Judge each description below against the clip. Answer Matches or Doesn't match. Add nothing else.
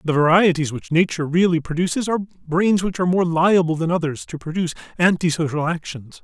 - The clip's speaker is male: Matches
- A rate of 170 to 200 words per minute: Matches